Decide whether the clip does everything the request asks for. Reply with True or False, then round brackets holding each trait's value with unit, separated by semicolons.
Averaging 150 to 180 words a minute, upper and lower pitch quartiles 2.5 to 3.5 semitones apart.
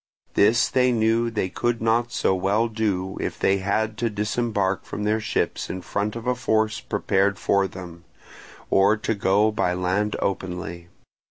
True (165 wpm; 2.8 semitones)